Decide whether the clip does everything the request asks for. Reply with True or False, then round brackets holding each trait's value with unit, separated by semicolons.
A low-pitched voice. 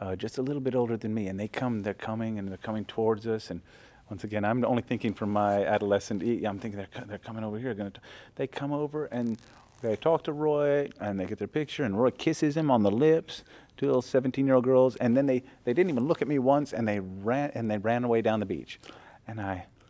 True (115 Hz)